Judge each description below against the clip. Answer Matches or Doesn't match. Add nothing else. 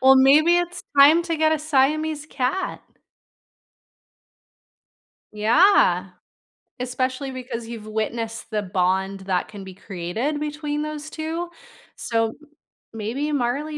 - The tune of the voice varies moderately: Doesn't match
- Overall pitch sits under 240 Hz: Doesn't match